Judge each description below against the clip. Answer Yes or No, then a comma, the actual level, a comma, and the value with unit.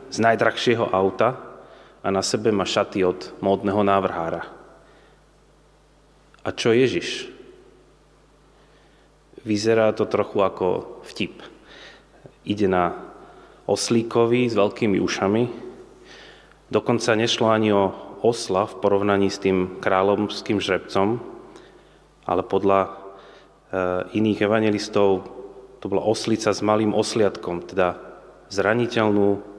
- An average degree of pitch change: No, narrow, 2.1 semitones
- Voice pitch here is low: Yes, low, 100 Hz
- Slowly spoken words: Yes, slow, 95 wpm